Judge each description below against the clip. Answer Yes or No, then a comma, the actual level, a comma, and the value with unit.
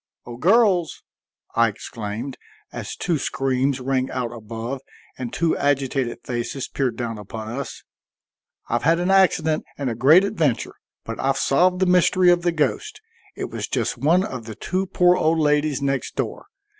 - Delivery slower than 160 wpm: No, average, 165 wpm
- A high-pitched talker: No, medium, 140 Hz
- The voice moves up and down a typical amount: No, wide, 5.8 semitones